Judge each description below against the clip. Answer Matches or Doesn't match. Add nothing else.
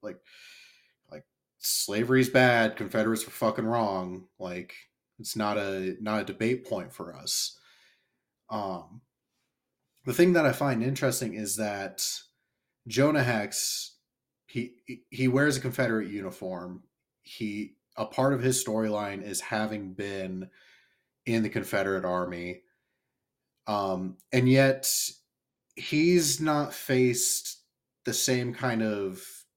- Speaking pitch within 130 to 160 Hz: Doesn't match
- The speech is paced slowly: Matches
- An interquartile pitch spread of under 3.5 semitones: Doesn't match